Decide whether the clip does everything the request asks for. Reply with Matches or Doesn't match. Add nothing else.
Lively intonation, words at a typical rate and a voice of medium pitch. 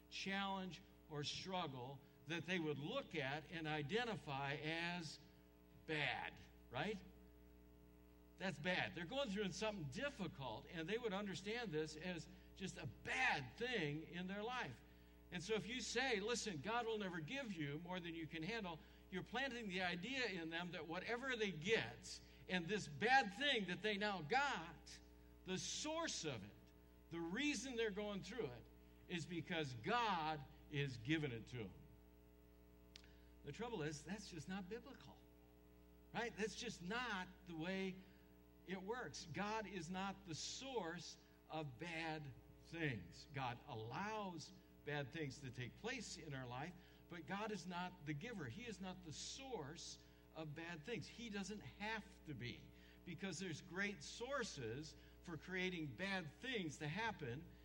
Matches